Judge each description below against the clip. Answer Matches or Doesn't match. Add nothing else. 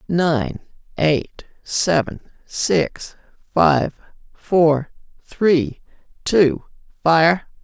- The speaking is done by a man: Doesn't match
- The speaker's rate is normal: Doesn't match